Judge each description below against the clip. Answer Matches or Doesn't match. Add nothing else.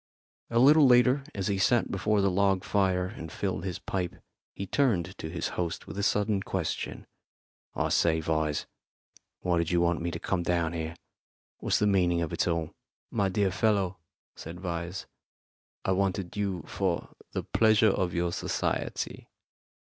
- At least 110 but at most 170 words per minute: Matches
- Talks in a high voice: Doesn't match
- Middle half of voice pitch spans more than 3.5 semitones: Doesn't match